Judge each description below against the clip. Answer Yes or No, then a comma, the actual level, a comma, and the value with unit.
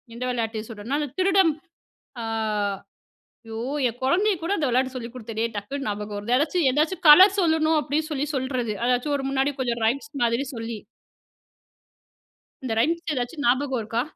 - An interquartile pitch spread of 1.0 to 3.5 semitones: No, average, 4.6 semitones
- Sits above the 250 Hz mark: Yes, very high, 260 Hz